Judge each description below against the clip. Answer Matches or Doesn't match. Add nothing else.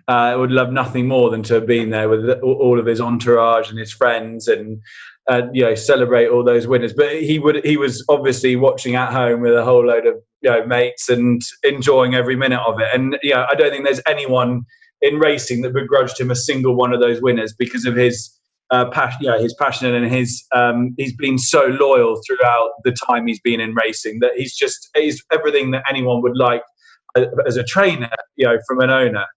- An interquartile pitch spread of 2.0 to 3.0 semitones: Matches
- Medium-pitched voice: Doesn't match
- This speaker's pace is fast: Matches